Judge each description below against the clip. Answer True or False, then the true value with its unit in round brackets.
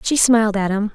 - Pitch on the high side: True (215 Hz)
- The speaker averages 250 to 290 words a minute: True (255 wpm)